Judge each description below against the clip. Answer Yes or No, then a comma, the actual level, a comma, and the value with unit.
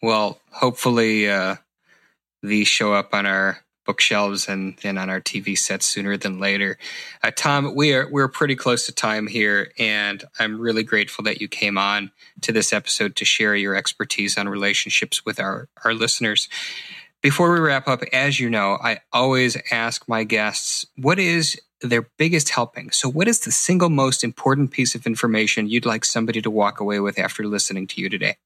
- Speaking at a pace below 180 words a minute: No, average, 185 wpm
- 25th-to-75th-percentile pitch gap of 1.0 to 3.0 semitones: No, average, 4.3 semitones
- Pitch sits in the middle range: No, low, 115 Hz